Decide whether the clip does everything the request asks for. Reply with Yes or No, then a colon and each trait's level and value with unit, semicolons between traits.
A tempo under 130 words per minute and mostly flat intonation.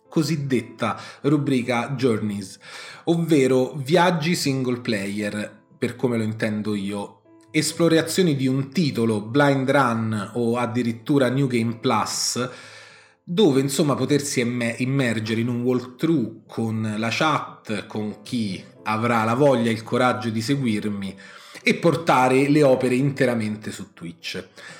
No: average, 120 wpm; average, 4.1 semitones